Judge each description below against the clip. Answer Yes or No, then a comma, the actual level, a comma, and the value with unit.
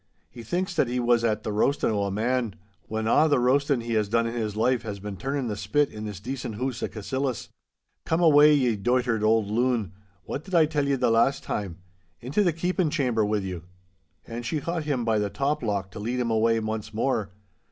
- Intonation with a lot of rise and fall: No, average, 4.3 semitones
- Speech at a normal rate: No, fast, 220 wpm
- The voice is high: No, low, 115 Hz